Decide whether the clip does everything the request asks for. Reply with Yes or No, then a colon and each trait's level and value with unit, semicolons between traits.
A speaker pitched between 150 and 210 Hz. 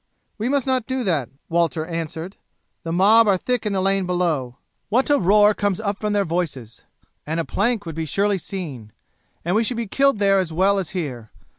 Yes: high, 190 Hz